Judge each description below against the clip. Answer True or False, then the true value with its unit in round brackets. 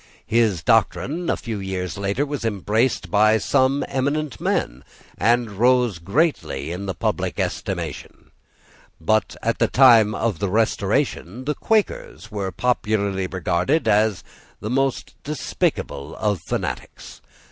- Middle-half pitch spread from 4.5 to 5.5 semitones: True (5.2 semitones)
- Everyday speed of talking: False (125 wpm)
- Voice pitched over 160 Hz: False (110 Hz)